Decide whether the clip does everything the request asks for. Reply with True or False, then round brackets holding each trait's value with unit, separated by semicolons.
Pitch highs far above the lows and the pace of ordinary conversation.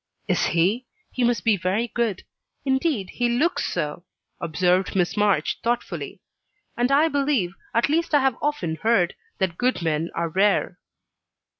True (6.4 semitones; 150 wpm)